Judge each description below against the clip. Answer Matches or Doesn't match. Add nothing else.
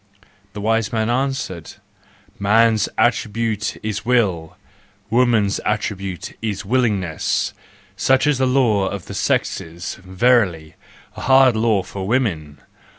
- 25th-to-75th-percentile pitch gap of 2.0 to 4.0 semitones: Matches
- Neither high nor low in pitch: Doesn't match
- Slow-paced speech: Matches